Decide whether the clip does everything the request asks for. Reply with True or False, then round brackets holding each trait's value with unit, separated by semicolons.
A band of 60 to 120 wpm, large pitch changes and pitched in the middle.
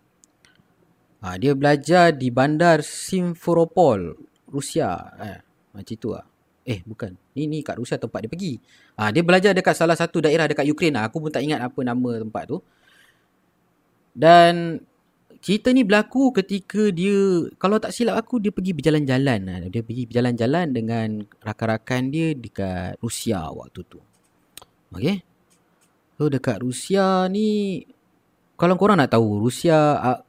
False (135 wpm; 7.6 semitones; 150 Hz)